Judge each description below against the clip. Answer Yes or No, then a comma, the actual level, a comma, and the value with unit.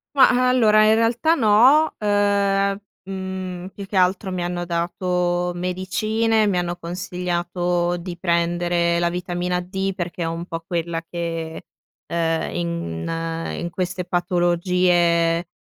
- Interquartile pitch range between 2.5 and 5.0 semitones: No, narrow, 2.1 semitones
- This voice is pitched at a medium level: Yes, medium, 180 Hz